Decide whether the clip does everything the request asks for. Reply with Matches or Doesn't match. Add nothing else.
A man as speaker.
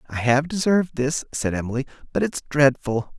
Matches